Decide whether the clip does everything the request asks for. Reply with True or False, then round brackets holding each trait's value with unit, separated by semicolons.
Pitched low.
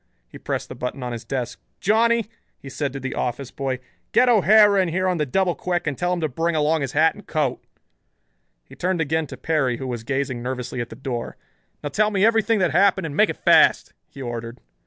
False (150 Hz)